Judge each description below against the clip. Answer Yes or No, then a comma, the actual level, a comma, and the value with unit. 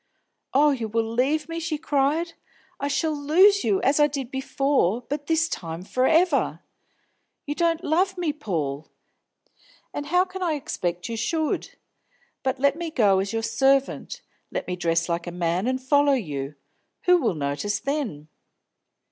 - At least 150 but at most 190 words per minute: Yes, average, 165 wpm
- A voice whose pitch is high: Yes, very high, 275 Hz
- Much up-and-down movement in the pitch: Yes, wide, 7.6 semitones